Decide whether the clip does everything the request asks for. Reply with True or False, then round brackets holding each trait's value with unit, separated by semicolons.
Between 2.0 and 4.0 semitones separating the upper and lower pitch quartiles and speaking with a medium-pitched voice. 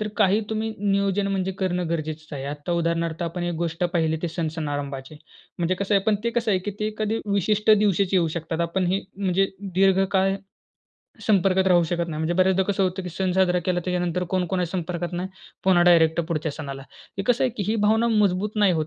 True (2.9 semitones; 180 Hz)